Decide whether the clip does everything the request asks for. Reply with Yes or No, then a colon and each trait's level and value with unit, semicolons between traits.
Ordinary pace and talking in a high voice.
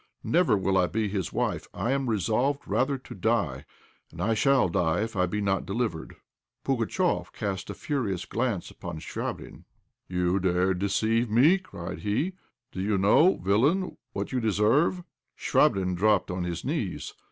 No: average, 160 wpm; low, 105 Hz